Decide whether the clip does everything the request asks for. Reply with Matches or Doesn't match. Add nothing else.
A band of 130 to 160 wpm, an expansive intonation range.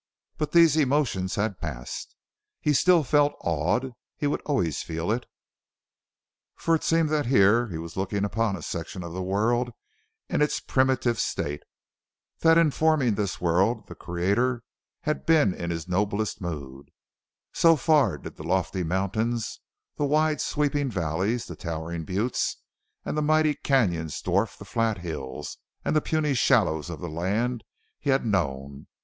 Matches